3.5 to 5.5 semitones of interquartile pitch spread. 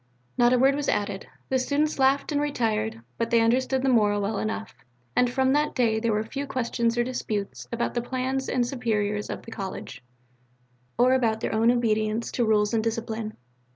No: average, 2.9 semitones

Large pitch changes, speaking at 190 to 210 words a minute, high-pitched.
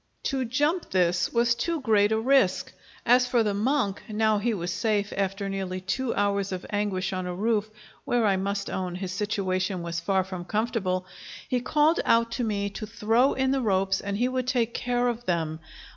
No: average, 4.1 semitones; average, 195 wpm; high, 210 Hz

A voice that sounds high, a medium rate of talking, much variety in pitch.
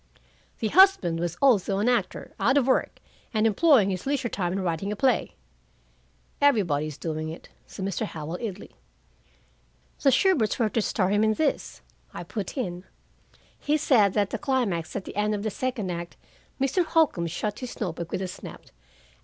Yes: high, 210 Hz; average, 180 wpm; wide, 6.3 semitones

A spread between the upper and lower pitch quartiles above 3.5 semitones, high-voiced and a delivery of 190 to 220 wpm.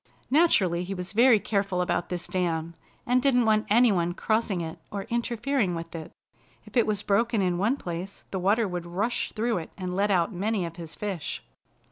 Yes: average, 4.2 semitones; high, 195 Hz; average, 195 wpm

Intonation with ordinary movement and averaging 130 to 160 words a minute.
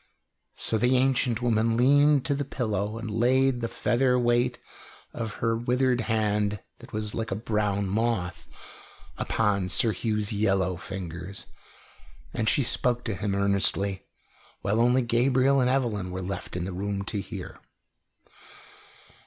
Yes: average, 3.5 semitones; average, 145 wpm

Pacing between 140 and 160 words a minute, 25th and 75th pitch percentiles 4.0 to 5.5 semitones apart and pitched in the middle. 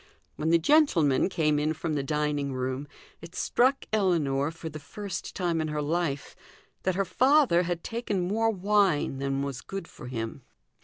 No: average, 170 wpm; average, 5.1 semitones; medium, 165 Hz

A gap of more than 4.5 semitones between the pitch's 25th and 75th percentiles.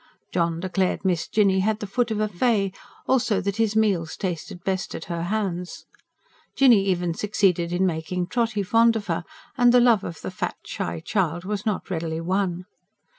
No: average, 3.6 semitones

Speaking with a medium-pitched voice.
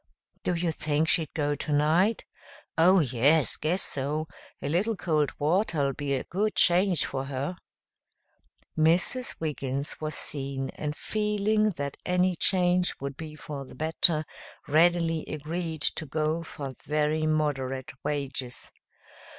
Yes: medium, 155 Hz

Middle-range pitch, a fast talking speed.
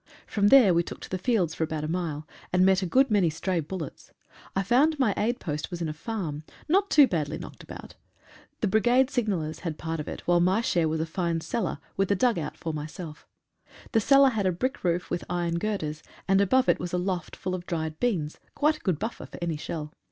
Yes: medium, 180 Hz; fast, 235 wpm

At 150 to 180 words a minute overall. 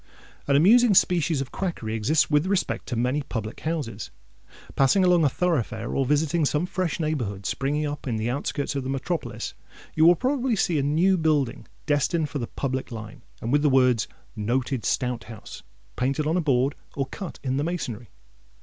Yes: average, 175 wpm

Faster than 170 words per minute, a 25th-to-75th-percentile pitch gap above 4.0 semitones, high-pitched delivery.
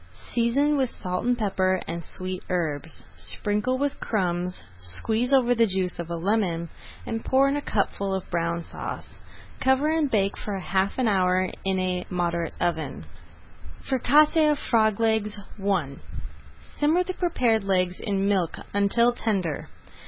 No: average, 155 wpm; average, 5.1 semitones; high, 200 Hz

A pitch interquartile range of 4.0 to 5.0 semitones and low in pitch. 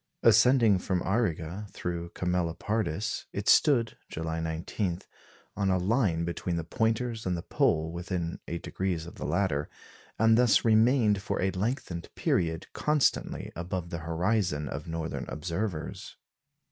Yes: average, 4.7 semitones; very low, 90 Hz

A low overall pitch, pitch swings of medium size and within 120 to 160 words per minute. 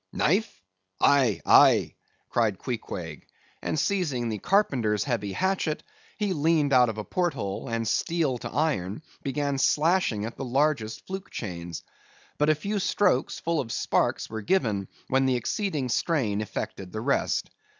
No: low, 130 Hz; wide, 6.7 semitones; average, 150 wpm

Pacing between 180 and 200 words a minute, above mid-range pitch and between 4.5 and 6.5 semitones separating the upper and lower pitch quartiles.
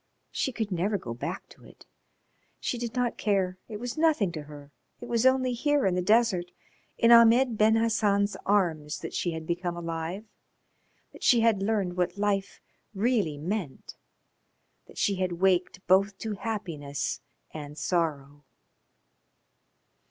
No: average, 150 wpm; high, 195 Hz; average, 4.8 semitones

